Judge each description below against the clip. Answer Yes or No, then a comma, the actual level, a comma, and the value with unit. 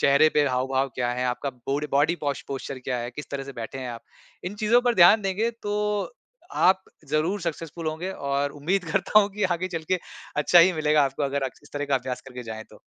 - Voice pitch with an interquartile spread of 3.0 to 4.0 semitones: No, average, 5.0 semitones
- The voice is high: No, medium, 145 Hz